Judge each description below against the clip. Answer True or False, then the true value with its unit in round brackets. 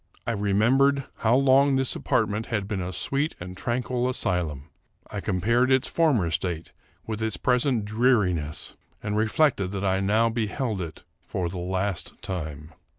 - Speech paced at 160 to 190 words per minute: False (150 wpm)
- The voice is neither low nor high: False (105 Hz)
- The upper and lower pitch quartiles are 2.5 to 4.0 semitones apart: False (5.4 semitones)